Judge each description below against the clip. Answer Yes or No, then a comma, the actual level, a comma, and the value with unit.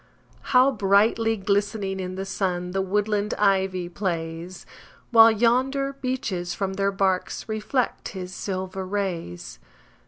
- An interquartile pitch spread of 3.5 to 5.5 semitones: No, average, 2.8 semitones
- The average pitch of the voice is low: No, high, 195 Hz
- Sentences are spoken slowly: Yes, slow, 120 wpm